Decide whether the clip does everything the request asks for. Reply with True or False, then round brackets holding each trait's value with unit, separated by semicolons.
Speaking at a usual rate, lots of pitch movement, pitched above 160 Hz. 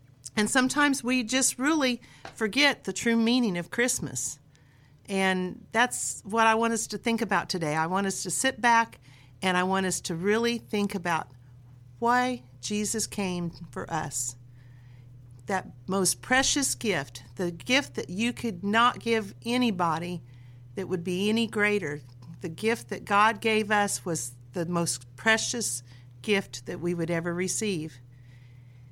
True (150 wpm; 8.9 semitones; 185 Hz)